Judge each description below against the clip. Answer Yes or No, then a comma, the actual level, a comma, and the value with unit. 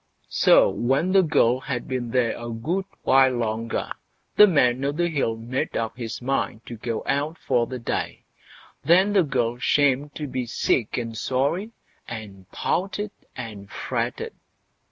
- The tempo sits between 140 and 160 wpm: Yes, average, 155 wpm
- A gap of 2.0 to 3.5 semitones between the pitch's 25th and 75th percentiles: No, average, 4.1 semitones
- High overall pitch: No, low, 130 Hz